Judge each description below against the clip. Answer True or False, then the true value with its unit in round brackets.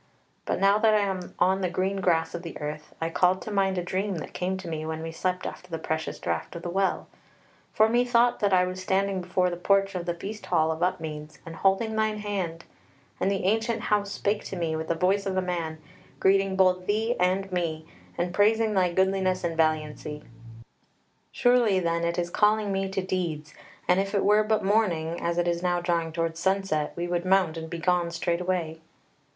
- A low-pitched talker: False (185 Hz)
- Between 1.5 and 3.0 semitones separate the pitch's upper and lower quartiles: True (2.7 semitones)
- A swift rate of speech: True (210 wpm)